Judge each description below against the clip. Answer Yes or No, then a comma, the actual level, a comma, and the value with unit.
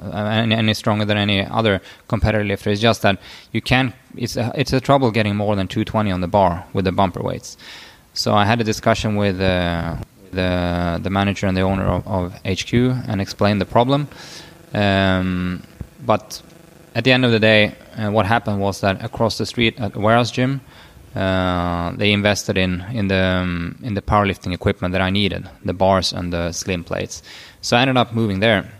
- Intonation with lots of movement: No, average, 3.3 semitones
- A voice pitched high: No, low, 105 Hz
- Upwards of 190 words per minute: Yes, average, 200 wpm